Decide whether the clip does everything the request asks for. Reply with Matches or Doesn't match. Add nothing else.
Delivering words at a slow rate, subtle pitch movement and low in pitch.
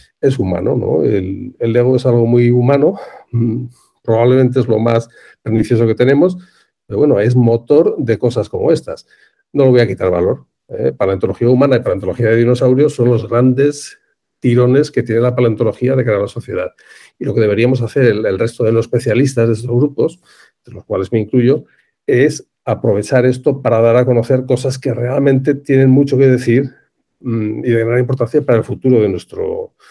Doesn't match